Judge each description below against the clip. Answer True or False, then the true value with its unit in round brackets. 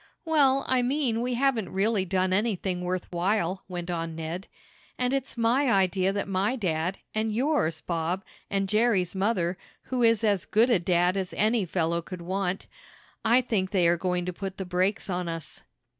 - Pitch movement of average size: True (4.2 semitones)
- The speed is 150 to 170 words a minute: False (180 wpm)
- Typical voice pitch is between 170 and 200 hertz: True (190 Hz)